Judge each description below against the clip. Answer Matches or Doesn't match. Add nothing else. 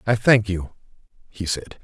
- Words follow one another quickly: Doesn't match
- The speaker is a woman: Doesn't match